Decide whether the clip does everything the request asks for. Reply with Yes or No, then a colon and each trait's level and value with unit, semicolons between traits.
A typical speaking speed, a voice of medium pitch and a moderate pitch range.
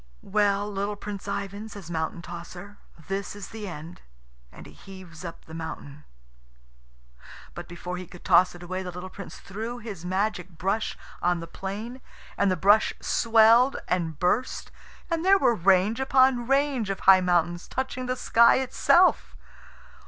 No: average, 160 wpm; high, 195 Hz; average, 4.0 semitones